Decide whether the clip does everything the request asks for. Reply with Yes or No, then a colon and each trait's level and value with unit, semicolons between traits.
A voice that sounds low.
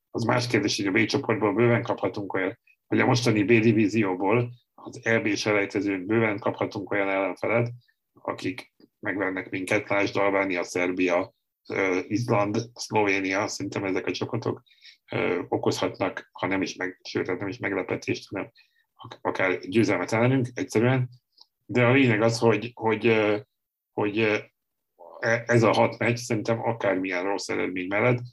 Yes: low, 115 Hz